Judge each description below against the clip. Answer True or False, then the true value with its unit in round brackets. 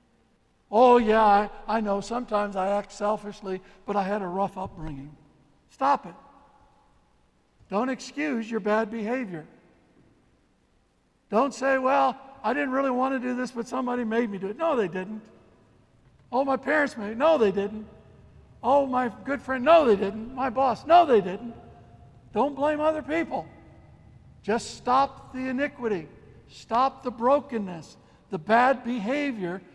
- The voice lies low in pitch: False (230 Hz)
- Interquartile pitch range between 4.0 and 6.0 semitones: True (4.8 semitones)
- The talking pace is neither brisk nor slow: True (150 wpm)